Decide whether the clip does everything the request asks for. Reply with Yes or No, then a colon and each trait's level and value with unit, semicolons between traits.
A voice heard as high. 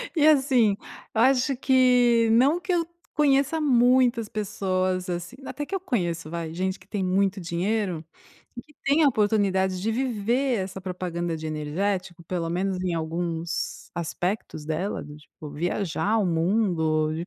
Yes: high, 195 Hz